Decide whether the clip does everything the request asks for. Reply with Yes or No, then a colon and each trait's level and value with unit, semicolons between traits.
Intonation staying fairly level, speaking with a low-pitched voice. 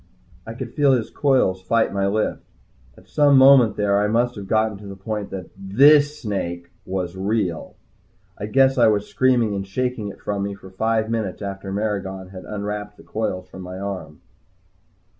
No: average, 3.0 semitones; low, 105 Hz